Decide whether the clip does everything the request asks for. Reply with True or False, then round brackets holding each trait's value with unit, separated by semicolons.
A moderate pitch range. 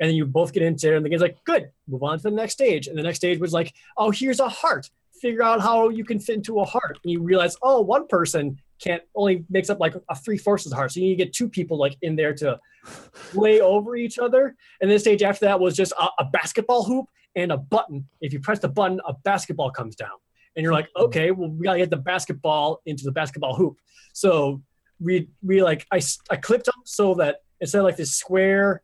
True (5.0 semitones)